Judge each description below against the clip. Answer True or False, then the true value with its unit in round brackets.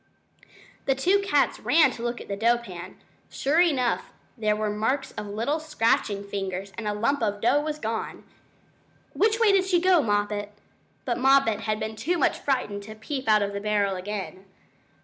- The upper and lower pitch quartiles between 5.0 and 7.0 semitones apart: True (5.5 semitones)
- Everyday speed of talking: True (185 wpm)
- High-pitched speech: True (225 Hz)